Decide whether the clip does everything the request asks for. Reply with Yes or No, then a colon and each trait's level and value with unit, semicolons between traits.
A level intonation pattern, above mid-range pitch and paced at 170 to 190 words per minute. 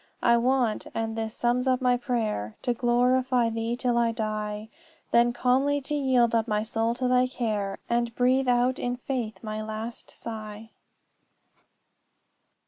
No: narrow, 2.1 semitones; high, 235 Hz; average, 150 wpm